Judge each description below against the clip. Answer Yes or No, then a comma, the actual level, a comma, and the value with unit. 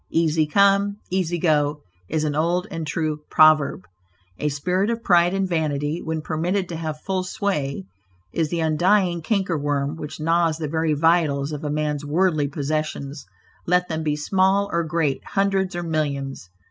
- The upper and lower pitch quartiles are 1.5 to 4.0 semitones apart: Yes, average, 3.1 semitones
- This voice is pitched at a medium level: Yes, medium, 160 Hz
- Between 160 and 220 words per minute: Yes, average, 165 wpm